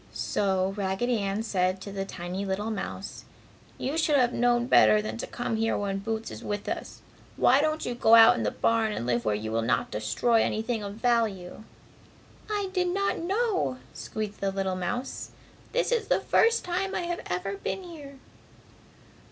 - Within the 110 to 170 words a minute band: No, average, 185 wpm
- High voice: Yes, high, 220 Hz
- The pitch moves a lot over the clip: Yes, wide, 5.8 semitones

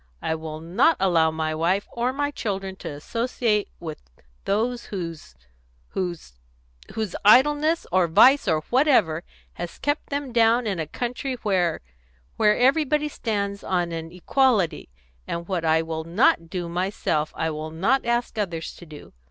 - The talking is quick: No, average, 150 wpm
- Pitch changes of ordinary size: No, wide, 6.7 semitones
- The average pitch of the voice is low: No, high, 190 Hz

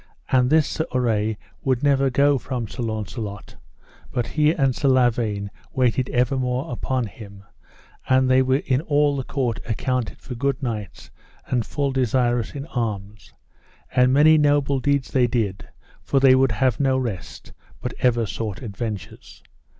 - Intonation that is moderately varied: Yes, average, 3.2 semitones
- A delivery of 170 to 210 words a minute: No, average, 155 wpm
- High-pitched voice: No, low, 125 Hz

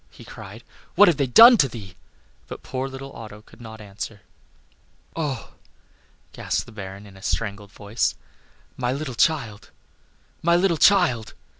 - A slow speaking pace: No, average, 150 wpm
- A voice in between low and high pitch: No, low, 120 Hz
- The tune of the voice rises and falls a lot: Yes, wide, 6.2 semitones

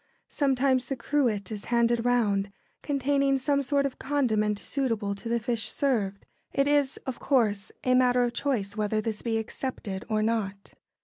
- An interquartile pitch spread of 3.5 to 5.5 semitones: Yes, average, 4.2 semitones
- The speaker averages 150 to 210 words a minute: Yes, average, 165 wpm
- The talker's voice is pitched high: Yes, high, 240 Hz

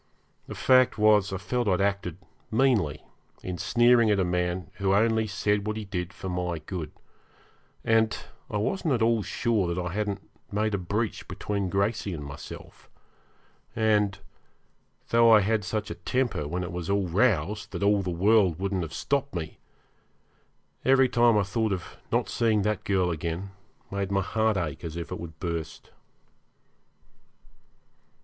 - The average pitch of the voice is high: No, low, 100 Hz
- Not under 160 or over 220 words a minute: Yes, average, 165 wpm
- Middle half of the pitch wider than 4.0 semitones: No, average, 3.7 semitones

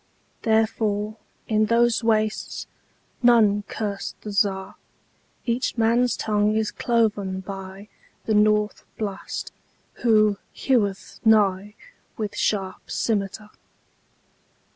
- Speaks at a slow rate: Yes, slow, 75 wpm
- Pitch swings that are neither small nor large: No, narrow, 1.8 semitones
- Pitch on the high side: Yes, high, 215 Hz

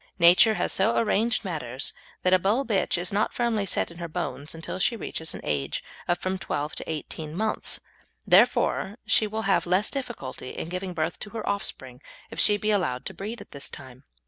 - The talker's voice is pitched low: No, medium, 185 Hz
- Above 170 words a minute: Yes, fast, 205 wpm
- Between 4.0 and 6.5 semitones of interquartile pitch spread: Yes, average, 4.9 semitones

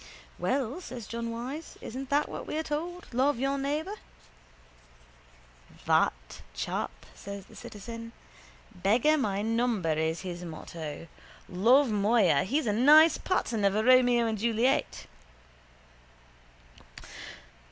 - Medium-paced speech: No, slow, 115 wpm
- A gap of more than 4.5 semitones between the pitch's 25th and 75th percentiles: Yes, wide, 5.6 semitones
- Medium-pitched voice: No, high, 235 Hz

